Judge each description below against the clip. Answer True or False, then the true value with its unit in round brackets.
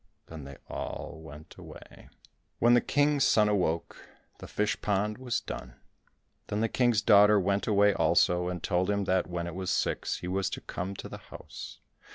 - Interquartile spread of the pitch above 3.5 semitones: False (3.0 semitones)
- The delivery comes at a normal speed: True (185 wpm)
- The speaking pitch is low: True (100 Hz)